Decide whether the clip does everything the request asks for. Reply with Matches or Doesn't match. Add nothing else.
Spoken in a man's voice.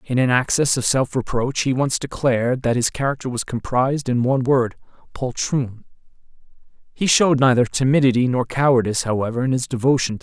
Matches